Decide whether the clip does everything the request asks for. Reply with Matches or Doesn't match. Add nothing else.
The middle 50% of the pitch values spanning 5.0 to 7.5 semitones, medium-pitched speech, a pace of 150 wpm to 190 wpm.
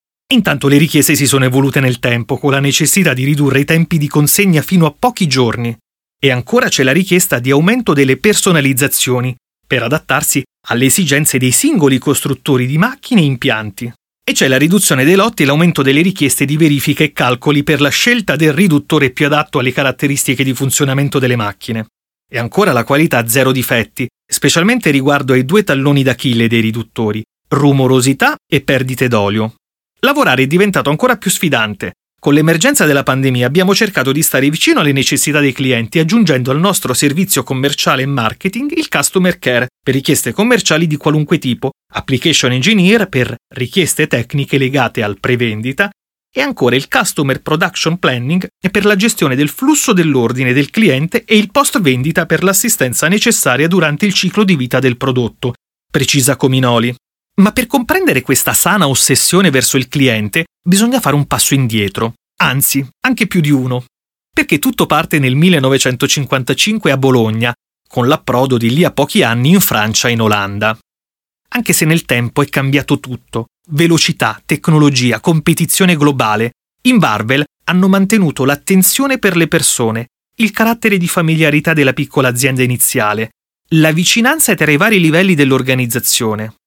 Matches